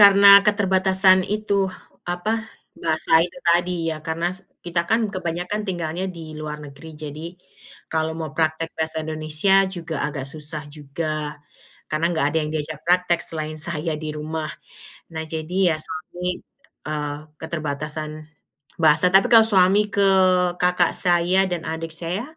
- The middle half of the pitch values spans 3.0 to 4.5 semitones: No, narrow, 2.6 semitones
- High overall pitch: No, medium, 165 Hz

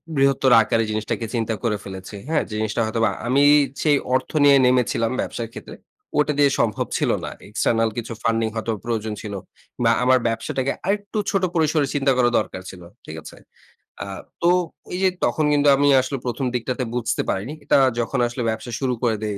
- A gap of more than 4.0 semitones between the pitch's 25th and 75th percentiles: No, average, 3.7 semitones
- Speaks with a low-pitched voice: Yes, low, 120 Hz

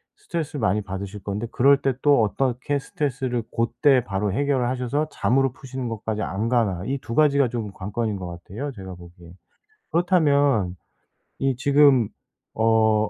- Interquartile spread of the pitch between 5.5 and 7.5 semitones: No, average, 5.1 semitones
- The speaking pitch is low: Yes, low, 120 Hz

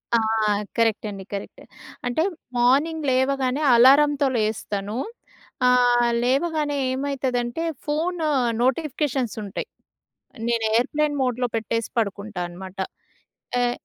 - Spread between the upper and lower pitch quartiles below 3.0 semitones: No, average, 4.1 semitones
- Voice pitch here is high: Yes, very high, 250 Hz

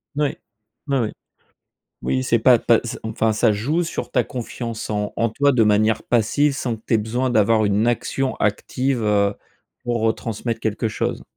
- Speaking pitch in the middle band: No, low, 115 Hz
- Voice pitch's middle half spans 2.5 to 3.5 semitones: Yes, average, 2.8 semitones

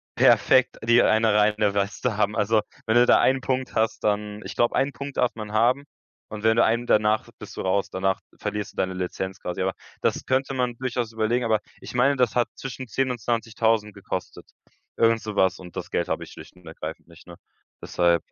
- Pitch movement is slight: No, average, 3.2 semitones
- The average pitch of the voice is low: Yes, low, 110 Hz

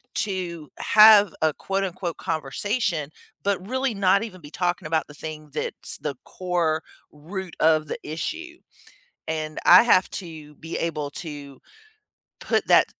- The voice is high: No, medium, 170 Hz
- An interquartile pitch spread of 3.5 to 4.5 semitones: Yes, average, 4.1 semitones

